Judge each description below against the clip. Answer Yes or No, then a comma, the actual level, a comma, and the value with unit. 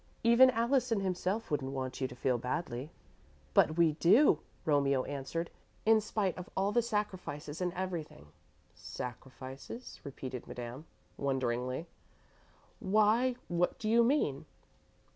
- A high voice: No, medium, 170 Hz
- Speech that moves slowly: Yes, slow, 125 wpm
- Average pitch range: No, wide, 8.3 semitones